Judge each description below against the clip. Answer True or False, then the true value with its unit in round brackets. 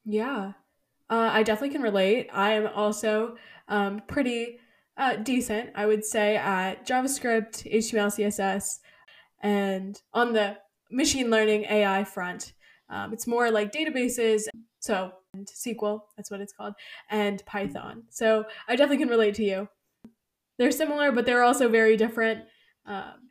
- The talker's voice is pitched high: True (220 Hz)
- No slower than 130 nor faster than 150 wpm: True (145 wpm)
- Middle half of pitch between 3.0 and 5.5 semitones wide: False (2.6 semitones)